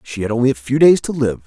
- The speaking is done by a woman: No, male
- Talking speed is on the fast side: Yes, fast, 325 wpm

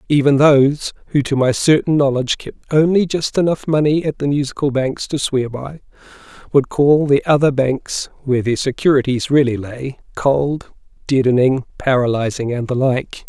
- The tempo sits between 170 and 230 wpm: No, average, 160 wpm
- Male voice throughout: Yes, male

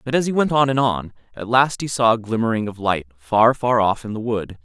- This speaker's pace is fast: Yes, fast, 270 wpm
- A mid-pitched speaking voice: No, low, 115 Hz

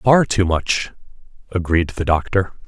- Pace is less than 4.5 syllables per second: Yes, 4.0 syllables/s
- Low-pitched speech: Yes, very low, 95 Hz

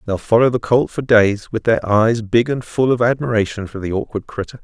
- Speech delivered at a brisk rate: Yes, fast, 235 wpm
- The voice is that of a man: Yes, male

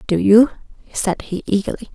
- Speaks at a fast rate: No, average, 155 wpm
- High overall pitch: Yes, high, 205 Hz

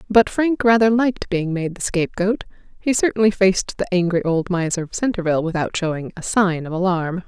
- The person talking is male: No, female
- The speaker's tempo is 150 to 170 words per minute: No, average, 190 wpm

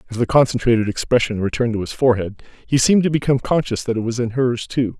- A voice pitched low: Yes, low, 120 Hz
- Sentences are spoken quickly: Yes, fast, 230 wpm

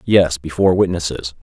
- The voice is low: Yes, very low, 85 Hz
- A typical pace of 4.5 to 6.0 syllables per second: Yes, 5.5 syllables/s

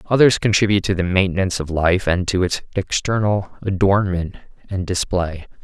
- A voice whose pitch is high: No, very low, 95 Hz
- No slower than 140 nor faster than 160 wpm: Yes, average, 150 wpm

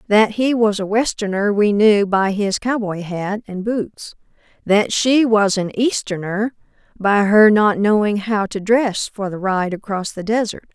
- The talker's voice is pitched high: Yes, high, 210 Hz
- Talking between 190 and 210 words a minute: No, average, 175 wpm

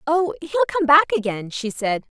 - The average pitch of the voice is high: Yes, very high, 275 Hz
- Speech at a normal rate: Yes, average, 190 wpm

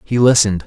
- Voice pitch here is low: Yes, low, 110 Hz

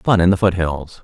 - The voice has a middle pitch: No, very low, 90 Hz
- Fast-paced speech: Yes, fast, 230 wpm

